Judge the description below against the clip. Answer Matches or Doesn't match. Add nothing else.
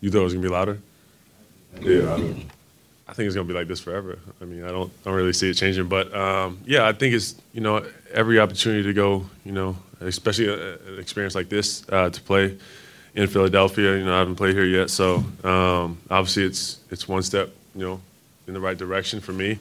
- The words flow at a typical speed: Doesn't match